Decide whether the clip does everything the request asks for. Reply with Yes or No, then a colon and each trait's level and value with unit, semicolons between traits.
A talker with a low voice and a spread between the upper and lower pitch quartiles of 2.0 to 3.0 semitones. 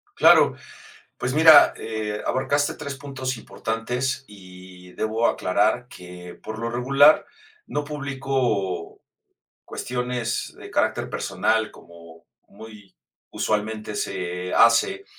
No: low, 115 Hz; average, 5.1 semitones